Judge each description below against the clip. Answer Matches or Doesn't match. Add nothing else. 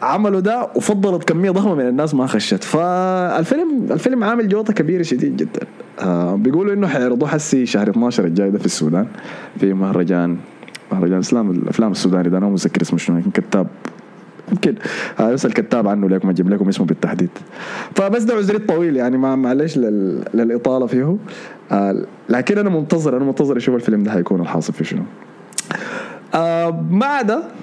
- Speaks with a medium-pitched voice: Matches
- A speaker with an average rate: Doesn't match